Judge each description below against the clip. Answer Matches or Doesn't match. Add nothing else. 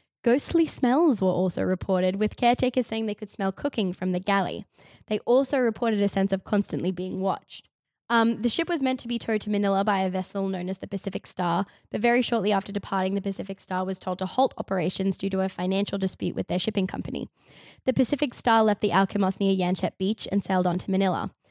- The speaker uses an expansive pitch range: Doesn't match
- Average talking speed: Doesn't match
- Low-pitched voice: Doesn't match